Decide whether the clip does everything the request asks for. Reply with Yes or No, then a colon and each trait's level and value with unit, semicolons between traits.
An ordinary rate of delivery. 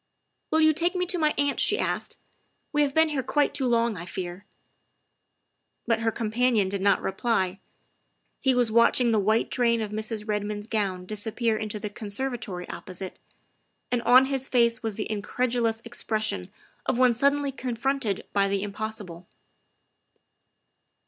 Yes: average, 160 wpm